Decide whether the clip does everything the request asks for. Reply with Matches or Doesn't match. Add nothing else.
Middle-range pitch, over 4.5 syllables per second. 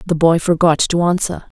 Matches